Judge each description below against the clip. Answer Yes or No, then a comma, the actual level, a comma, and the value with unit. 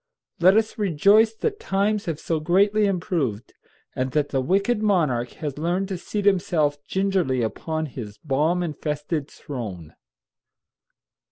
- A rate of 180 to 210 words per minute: No, slow, 135 wpm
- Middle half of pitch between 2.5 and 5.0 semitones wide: No, wide, 5.5 semitones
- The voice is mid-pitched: Yes, medium, 165 Hz